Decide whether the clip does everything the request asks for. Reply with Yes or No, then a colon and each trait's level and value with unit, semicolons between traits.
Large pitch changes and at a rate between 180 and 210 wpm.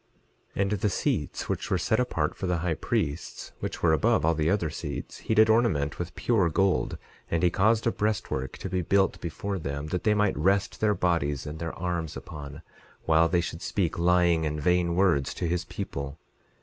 No: average, 3.7 semitones; average, 200 wpm